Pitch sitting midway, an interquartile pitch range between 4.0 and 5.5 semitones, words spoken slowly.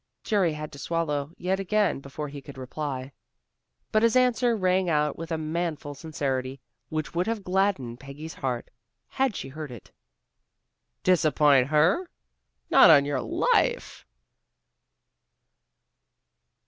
Yes: medium, 155 Hz; average, 5.2 semitones; slow, 125 wpm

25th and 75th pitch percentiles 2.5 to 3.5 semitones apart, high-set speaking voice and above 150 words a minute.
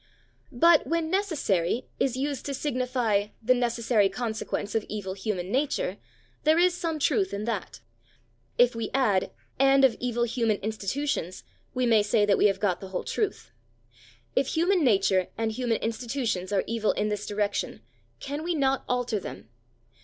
No: average, 4.9 semitones; high, 235 Hz; average, 160 wpm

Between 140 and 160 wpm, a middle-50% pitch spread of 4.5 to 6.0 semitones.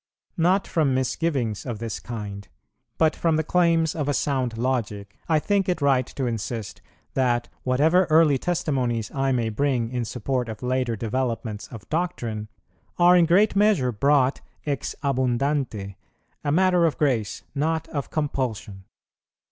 Yes: average, 150 wpm; average, 5.3 semitones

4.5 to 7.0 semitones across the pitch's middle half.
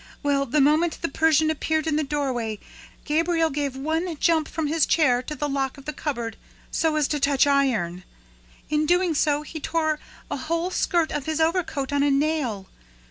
No: narrow, 2.4 semitones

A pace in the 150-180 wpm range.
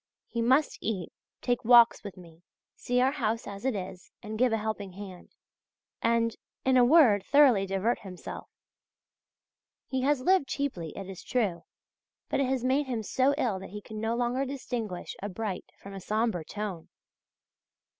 Yes: average, 170 wpm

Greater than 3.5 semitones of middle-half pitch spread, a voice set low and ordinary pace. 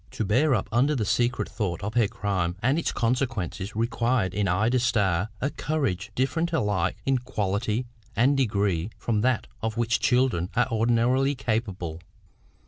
Yes: average, 4.1 semitones; low, 115 Hz; average, 155 wpm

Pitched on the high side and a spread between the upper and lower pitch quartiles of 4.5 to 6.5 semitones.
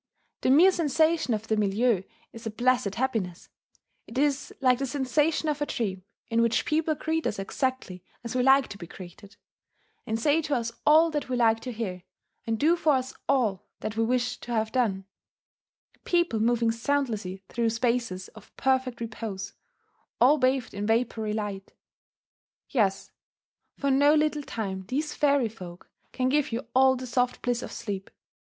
No: high, 245 Hz; average, 4.1 semitones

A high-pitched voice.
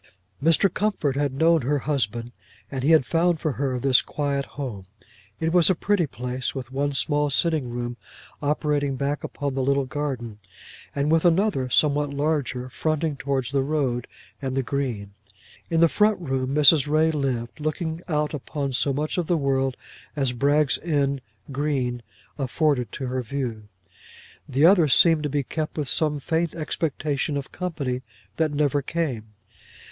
No: medium, 140 Hz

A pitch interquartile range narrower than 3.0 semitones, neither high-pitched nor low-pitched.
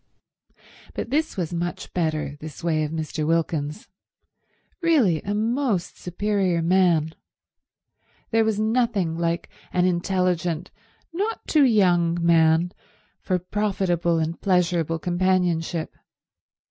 No: average, 3.5 semitones; medium, 175 Hz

